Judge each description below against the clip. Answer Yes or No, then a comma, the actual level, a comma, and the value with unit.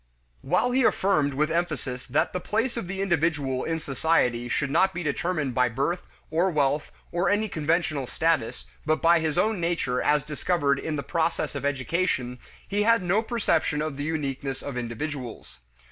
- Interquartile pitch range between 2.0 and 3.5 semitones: No, average, 4.2 semitones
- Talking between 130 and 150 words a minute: No, average, 175 wpm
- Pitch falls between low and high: Yes, medium, 155 Hz